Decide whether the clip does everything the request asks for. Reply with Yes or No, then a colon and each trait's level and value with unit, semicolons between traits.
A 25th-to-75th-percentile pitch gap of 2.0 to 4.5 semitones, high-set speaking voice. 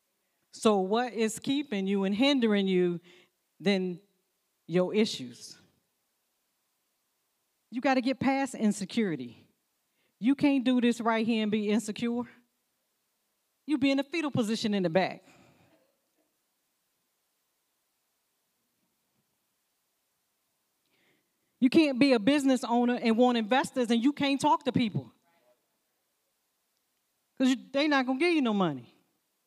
No: average, 5.1 semitones; high, 235 Hz